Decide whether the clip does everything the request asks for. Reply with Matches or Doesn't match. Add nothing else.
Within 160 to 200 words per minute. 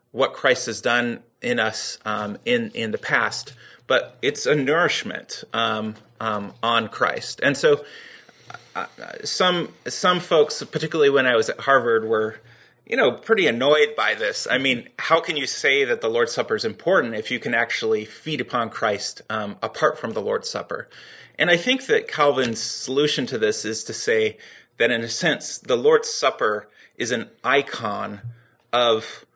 Matches